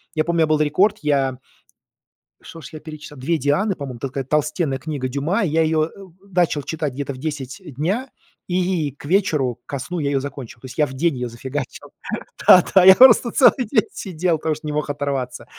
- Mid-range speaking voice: Yes, medium, 150 Hz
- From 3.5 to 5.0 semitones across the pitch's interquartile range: Yes, average, 3.8 semitones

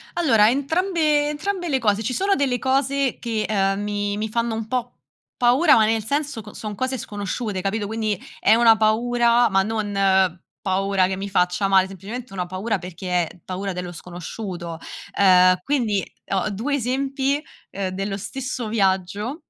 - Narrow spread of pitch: No, average, 4.6 semitones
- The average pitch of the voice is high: Yes, high, 215 Hz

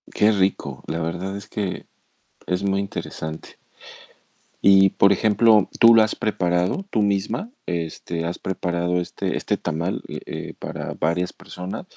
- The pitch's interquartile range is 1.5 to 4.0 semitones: Yes, narrow, 2.6 semitones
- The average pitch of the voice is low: Yes, very low, 95 Hz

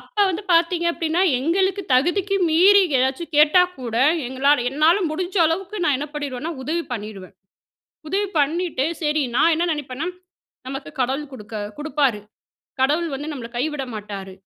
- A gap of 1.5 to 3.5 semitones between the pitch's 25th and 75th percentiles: No, average, 4.7 semitones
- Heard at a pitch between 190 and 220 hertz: No, very high, 300 Hz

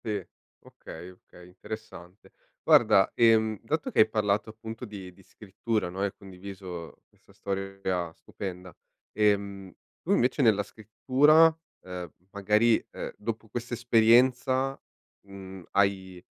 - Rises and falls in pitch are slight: No, average, 3.0 semitones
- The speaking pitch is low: Yes, low, 100 Hz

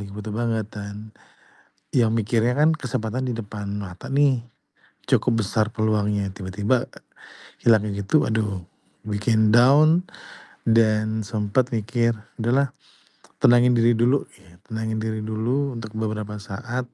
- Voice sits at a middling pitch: No, low, 110 Hz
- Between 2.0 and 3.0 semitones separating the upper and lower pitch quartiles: Yes, narrow, 2.4 semitones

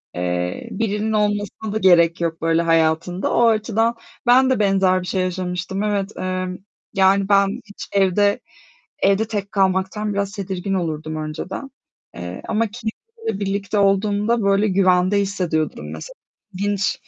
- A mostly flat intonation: Yes, narrow, 2.3 semitones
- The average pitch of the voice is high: Yes, high, 195 Hz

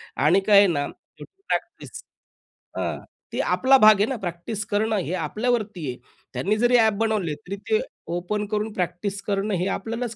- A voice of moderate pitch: No, high, 205 Hz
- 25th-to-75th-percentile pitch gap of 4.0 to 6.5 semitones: No, average, 3.5 semitones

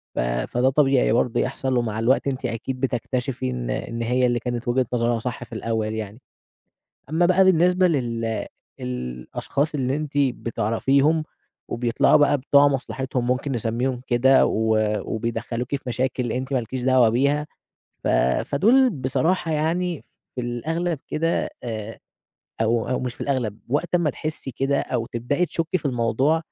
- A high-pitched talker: No, low, 130 Hz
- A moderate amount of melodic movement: Yes, average, 3.7 semitones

